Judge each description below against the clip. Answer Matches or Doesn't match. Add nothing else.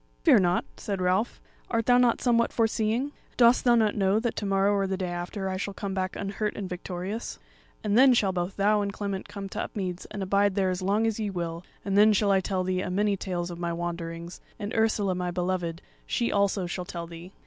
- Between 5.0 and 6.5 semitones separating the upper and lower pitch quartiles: Doesn't match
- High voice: Matches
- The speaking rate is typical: Doesn't match